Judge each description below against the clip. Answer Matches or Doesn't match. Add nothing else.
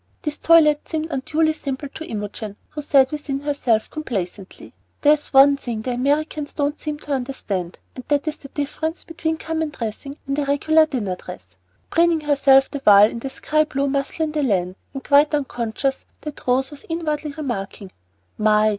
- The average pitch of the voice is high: Matches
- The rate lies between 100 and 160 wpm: Doesn't match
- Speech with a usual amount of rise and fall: Matches